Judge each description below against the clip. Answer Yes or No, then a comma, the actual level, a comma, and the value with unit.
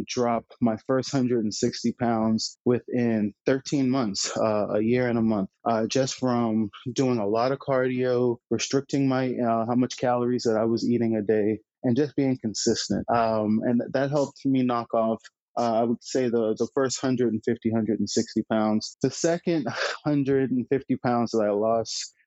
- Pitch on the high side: No, low, 120 Hz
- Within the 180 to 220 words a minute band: No, average, 165 wpm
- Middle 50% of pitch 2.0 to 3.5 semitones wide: Yes, average, 2.7 semitones